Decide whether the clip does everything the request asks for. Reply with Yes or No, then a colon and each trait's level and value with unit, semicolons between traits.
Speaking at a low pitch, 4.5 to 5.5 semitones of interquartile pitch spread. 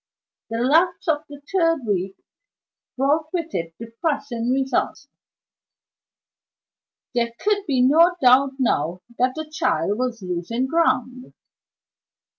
No: very high, 260 Hz; average, 5.2 semitones